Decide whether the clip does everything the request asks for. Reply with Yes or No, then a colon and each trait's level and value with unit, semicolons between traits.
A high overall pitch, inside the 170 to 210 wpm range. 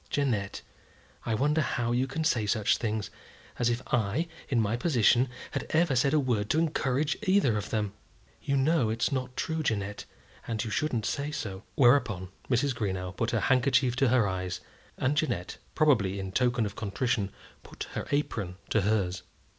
No: low, 120 Hz; average, 175 wpm